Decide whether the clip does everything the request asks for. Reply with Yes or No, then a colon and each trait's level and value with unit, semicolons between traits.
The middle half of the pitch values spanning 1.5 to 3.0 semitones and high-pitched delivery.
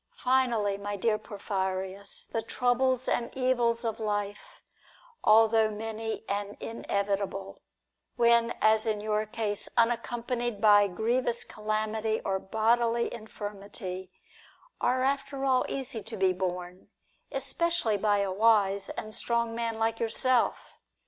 Yes: narrow, 2.5 semitones; high, 220 Hz